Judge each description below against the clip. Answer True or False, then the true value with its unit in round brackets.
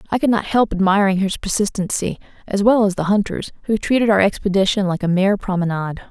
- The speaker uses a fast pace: False (195 wpm)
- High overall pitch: True (200 Hz)